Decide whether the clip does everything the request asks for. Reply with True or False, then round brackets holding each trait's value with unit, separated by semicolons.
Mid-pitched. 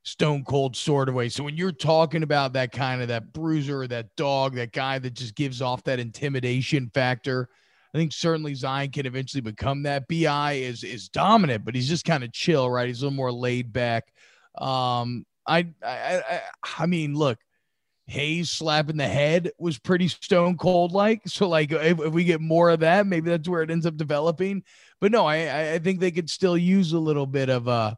True (145 Hz)